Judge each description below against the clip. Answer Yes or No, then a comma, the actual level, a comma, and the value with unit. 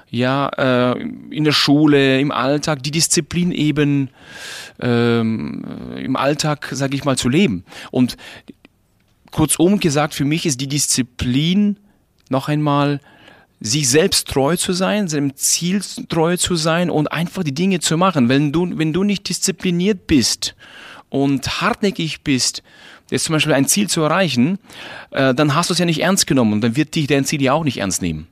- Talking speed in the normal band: Yes, average, 165 wpm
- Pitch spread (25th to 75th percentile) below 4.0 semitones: No, average, 4.5 semitones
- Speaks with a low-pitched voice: No, medium, 150 Hz